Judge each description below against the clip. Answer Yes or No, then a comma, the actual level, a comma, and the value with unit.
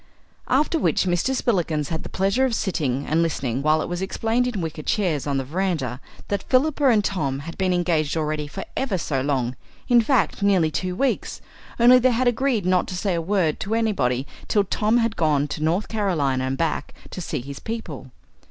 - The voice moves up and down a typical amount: No, wide, 6.7 semitones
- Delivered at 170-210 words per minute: Yes, average, 200 wpm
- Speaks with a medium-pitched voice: Yes, medium, 180 Hz